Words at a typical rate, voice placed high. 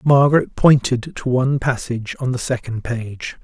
No: average, 155 wpm; low, 125 Hz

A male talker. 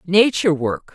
No: female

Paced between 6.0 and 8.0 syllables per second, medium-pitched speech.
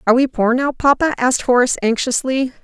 No: 6.4 syllables/s; very high, 255 Hz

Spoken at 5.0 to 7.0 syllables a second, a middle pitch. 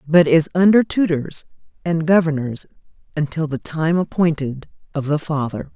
No: 4.8 syllables/s; medium, 155 Hz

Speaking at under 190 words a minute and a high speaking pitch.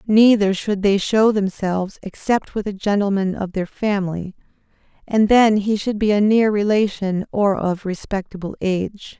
Yes: average, 155 wpm; high, 200 Hz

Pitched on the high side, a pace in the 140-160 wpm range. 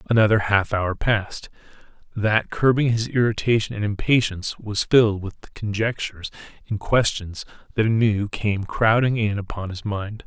No: low, 105 Hz; average, 145 wpm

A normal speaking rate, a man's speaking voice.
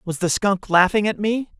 No: fast, 225 wpm; male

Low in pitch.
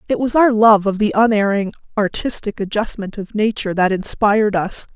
No: high, 210 Hz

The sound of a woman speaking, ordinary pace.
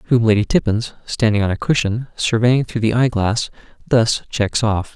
No: male; average, 180 wpm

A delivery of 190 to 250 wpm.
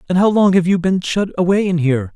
No: fast, 280 wpm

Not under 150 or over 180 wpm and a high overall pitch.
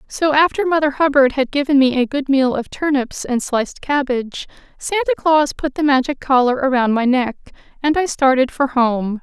No: average, 190 wpm; very high, 270 Hz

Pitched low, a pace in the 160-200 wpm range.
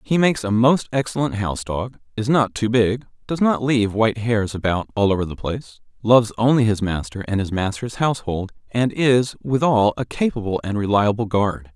Yes: low, 110 Hz; average, 190 wpm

